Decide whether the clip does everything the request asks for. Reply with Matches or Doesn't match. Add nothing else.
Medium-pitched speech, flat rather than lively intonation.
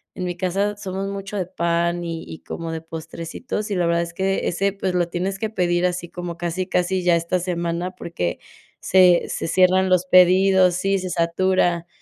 Matches